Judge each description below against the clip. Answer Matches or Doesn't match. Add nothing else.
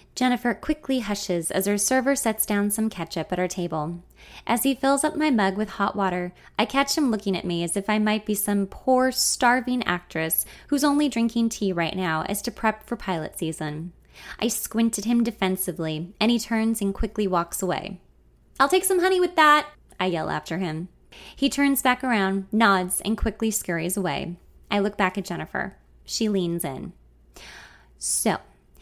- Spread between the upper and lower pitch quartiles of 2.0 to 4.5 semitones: Doesn't match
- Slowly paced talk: Doesn't match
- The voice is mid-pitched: Doesn't match